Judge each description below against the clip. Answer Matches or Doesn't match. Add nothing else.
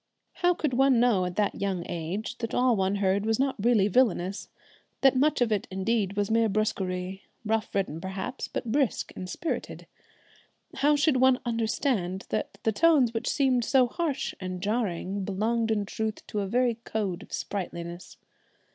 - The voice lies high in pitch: Matches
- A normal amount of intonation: Matches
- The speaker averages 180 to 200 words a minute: Doesn't match